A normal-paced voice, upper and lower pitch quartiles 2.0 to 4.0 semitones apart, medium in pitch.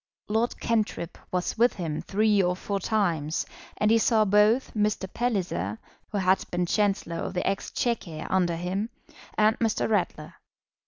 No: average, 150 wpm; average, 3.5 semitones; high, 200 Hz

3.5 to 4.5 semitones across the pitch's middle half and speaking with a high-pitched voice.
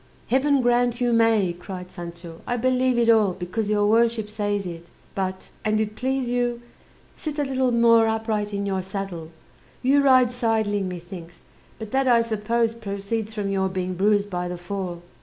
Yes: average, 3.8 semitones; high, 215 Hz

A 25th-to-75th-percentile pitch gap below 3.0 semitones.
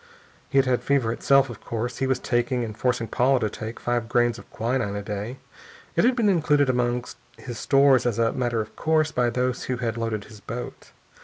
Yes: narrow, 2.5 semitones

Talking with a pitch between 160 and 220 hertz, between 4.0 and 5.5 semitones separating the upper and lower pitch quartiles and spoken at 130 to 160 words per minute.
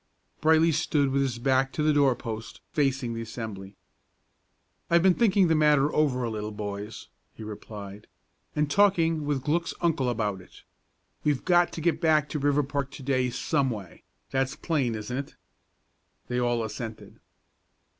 No: low, 135 Hz; average, 5.1 semitones; average, 155 wpm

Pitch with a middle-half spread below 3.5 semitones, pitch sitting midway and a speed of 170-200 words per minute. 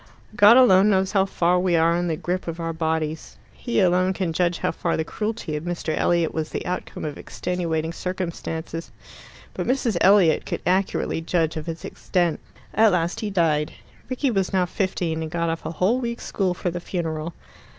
Yes: average, 2.7 semitones; medium, 175 Hz; average, 190 wpm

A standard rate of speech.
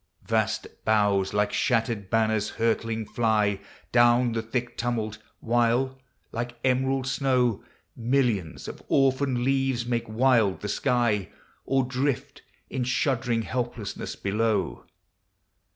No: slow, 110 wpm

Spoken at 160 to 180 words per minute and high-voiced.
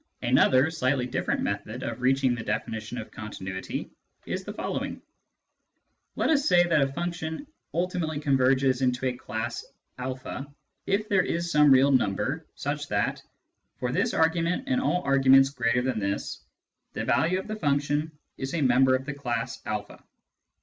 No: average, 165 wpm; low, 135 Hz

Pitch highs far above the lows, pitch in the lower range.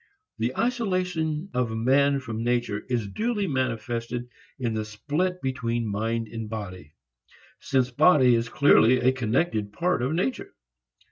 No: average, 4.7 semitones; low, 125 Hz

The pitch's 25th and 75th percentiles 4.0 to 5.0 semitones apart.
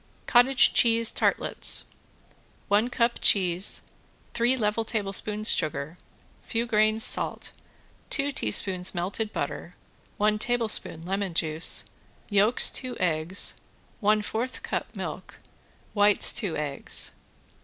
Yes: average, 4.3 semitones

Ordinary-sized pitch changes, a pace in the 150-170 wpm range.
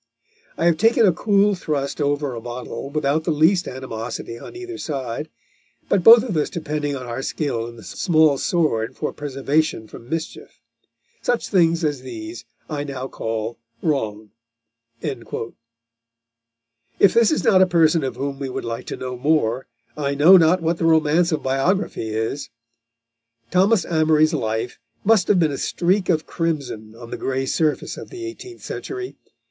No: wide, 6.0 semitones; average, 165 wpm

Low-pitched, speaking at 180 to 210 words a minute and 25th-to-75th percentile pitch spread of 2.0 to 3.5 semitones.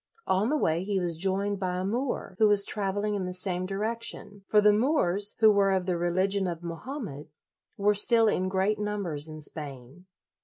No: high, 195 Hz; average, 190 wpm; narrow, 2.6 semitones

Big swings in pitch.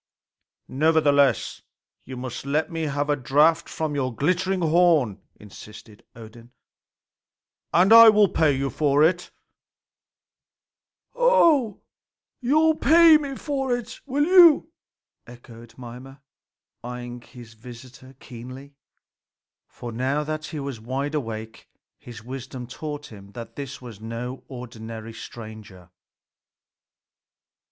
Yes: wide, 5.7 semitones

